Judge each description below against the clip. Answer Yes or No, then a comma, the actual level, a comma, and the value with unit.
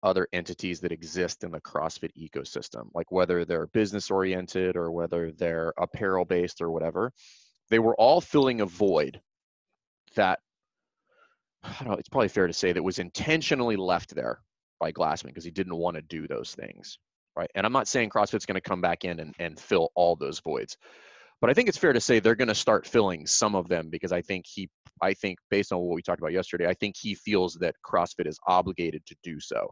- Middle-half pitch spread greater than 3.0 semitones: No, average, 2.7 semitones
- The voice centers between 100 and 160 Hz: No, very low, 90 Hz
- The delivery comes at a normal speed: No, fast, 215 wpm